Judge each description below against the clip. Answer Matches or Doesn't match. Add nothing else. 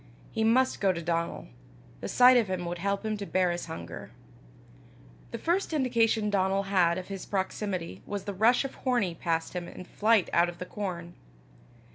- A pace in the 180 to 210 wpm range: Matches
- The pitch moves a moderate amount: Matches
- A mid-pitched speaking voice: Doesn't match